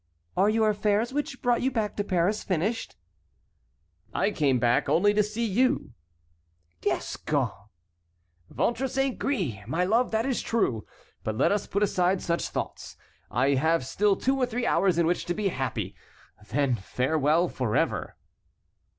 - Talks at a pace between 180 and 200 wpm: No, average, 150 wpm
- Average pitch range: No, wide, 7.3 semitones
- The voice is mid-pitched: No, high, 195 Hz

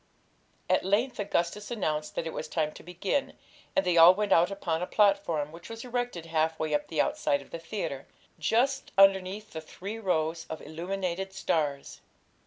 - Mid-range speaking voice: Yes, medium, 180 Hz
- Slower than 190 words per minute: Yes, average, 180 wpm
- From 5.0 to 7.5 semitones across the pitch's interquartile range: No, average, 4.2 semitones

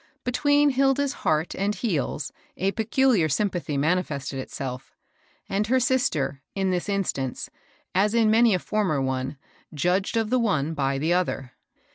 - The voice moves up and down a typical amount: No, wide, 7.9 semitones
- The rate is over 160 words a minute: No, average, 145 wpm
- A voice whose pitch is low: No, medium, 185 Hz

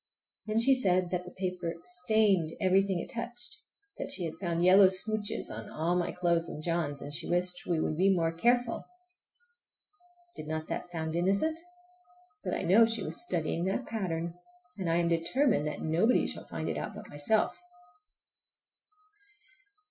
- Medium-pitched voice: Yes, medium, 180 Hz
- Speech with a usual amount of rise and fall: Yes, average, 3.8 semitones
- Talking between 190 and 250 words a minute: No, average, 165 wpm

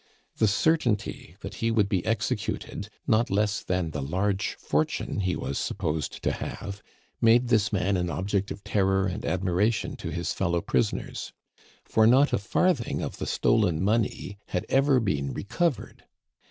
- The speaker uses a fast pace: No, average, 155 wpm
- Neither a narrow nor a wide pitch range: Yes, average, 3.6 semitones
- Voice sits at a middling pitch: No, low, 100 Hz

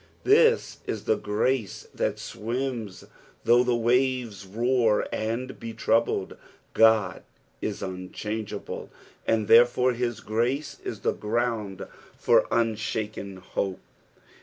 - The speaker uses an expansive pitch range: No, average, 2.7 semitones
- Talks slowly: Yes, slow, 110 wpm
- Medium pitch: No, low, 115 Hz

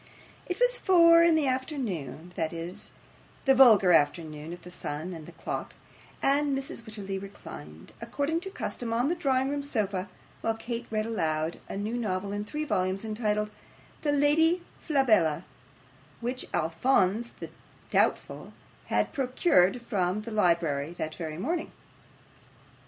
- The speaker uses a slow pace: No, average, 145 wpm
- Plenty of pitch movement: Yes, wide, 7.4 semitones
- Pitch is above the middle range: Yes, high, 215 Hz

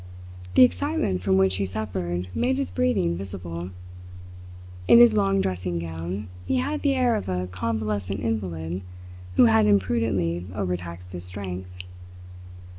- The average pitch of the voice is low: Yes, very low, 95 Hz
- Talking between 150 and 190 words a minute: No, slow, 135 wpm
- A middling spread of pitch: Yes, average, 4.1 semitones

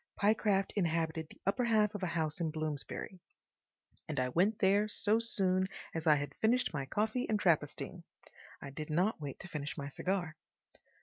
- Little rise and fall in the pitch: No, average, 5.0 semitones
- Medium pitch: Yes, medium, 175 Hz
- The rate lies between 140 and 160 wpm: No, average, 175 wpm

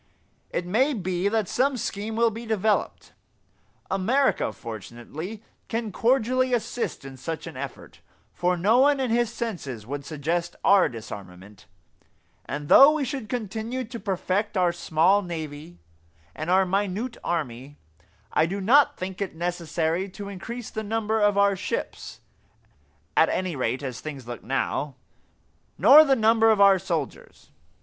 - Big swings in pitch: Yes, wide, 6.1 semitones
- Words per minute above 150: No, average, 145 wpm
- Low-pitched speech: No, high, 190 Hz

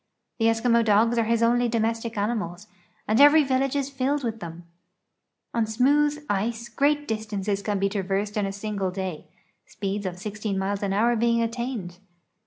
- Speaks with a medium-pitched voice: No, high, 220 Hz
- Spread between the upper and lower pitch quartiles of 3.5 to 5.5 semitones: No, average, 3.0 semitones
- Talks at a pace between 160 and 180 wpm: Yes, average, 170 wpm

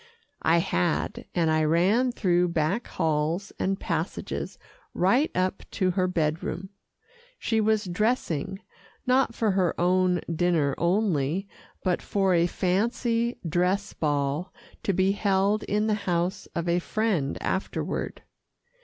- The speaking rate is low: Yes, slow, 130 wpm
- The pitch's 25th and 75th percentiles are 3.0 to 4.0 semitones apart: Yes, average, 3.3 semitones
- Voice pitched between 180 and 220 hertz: Yes, medium, 185 Hz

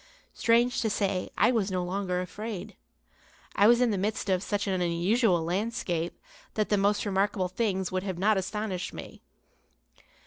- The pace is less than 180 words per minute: Yes, average, 165 wpm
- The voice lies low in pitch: No, high, 200 Hz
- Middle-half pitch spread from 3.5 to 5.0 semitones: No, average, 2.8 semitones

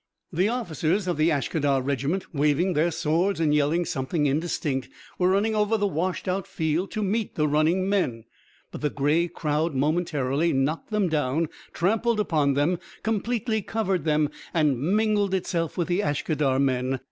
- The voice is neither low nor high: Yes, medium, 165 Hz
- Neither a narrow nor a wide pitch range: Yes, average, 4.7 semitones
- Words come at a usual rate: Yes, average, 160 wpm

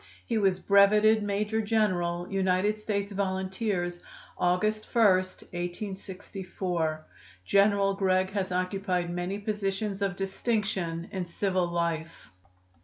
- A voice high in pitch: Yes, high, 195 Hz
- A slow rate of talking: Yes, slow, 105 wpm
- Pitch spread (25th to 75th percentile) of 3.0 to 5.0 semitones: No, narrow, 2.4 semitones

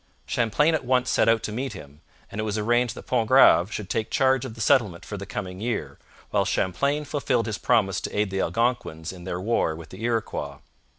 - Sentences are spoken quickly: Yes, fast, 215 wpm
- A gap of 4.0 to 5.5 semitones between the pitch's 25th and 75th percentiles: Yes, average, 4.3 semitones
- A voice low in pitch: Yes, low, 110 Hz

